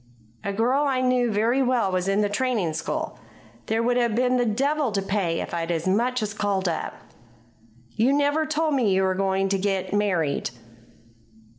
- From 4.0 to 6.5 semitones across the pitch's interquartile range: Yes, average, 4.8 semitones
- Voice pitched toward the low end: No, high, 210 Hz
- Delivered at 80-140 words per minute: No, average, 185 wpm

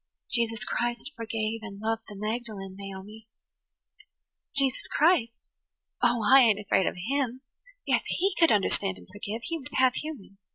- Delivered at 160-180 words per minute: No, average, 150 wpm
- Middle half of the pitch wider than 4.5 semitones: No, average, 3.9 semitones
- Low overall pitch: No, high, 225 Hz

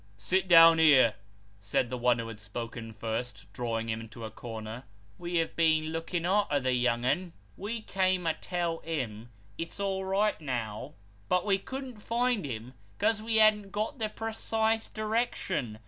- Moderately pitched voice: Yes, medium, 165 Hz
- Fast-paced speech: No, average, 170 wpm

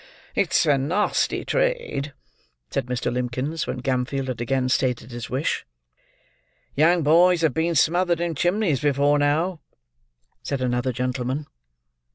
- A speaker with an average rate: No, slow, 130 wpm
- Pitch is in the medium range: Yes, medium, 145 Hz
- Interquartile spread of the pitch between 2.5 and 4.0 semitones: No, average, 4.8 semitones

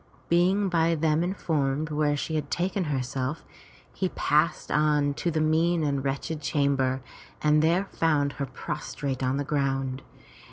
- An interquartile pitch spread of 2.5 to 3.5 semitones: Yes, average, 2.8 semitones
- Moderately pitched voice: Yes, medium, 150 Hz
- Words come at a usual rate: Yes, average, 150 wpm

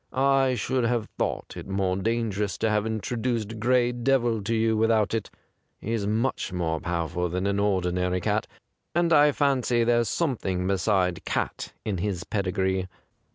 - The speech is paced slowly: No, average, 160 wpm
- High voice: No, low, 110 Hz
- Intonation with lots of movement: No, average, 4.2 semitones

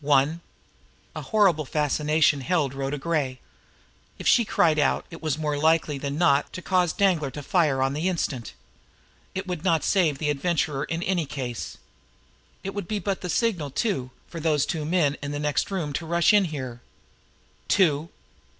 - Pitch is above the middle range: No, medium, 155 Hz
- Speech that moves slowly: No, average, 175 wpm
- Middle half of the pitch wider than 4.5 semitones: No, average, 3.7 semitones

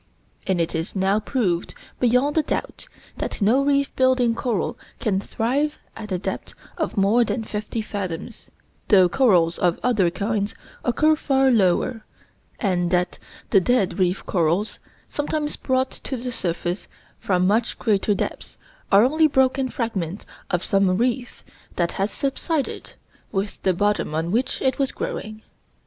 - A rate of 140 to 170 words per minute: Yes, average, 150 wpm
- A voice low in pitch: No, high, 215 Hz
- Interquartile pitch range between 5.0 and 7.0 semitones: Yes, wide, 5.6 semitones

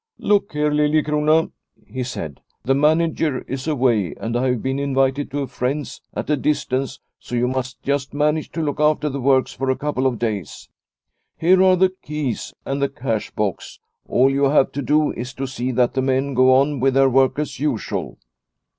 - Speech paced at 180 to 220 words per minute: Yes, average, 200 wpm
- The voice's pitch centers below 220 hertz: Yes, low, 135 Hz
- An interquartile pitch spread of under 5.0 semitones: Yes, narrow, 2.6 semitones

